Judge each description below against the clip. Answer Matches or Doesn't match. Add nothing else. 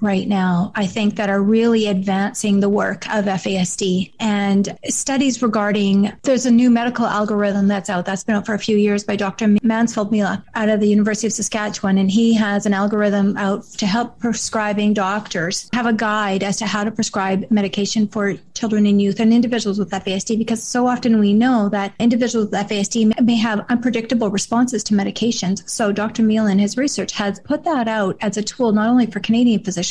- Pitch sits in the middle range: Doesn't match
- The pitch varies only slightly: Matches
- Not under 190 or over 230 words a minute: Matches